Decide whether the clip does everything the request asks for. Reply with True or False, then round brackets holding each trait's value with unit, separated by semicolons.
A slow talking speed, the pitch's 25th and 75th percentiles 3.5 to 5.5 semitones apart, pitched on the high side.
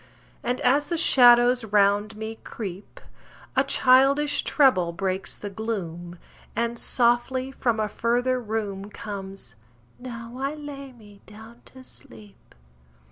True (125 wpm; 4.0 semitones; 230 Hz)